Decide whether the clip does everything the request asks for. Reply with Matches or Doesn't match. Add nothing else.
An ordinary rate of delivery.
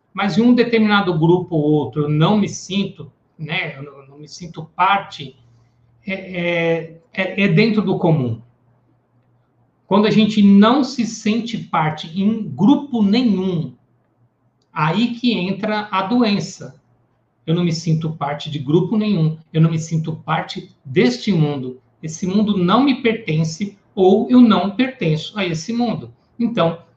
Matches